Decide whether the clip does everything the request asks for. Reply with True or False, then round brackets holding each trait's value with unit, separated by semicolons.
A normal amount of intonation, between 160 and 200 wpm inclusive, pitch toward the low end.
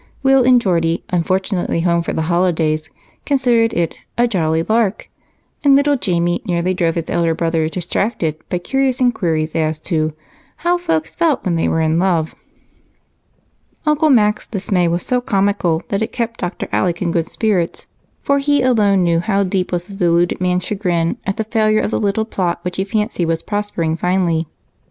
False (4.7 semitones; 175 wpm; 185 Hz)